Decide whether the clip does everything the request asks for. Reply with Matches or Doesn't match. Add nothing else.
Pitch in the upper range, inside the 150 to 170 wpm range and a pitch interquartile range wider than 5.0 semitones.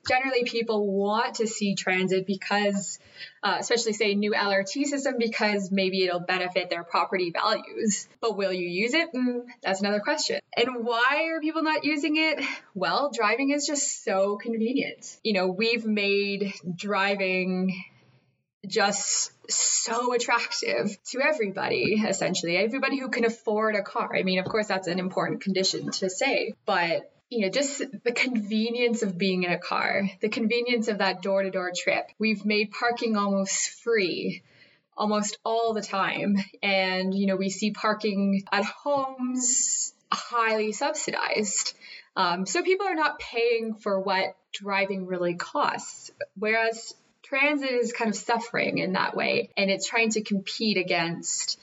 Doesn't match